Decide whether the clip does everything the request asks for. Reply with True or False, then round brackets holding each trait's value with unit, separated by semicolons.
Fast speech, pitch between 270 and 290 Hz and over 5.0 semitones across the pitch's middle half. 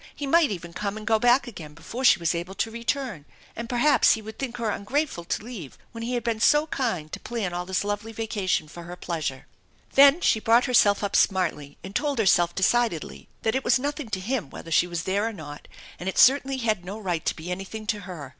False (230 wpm; 210 Hz; 5.4 semitones)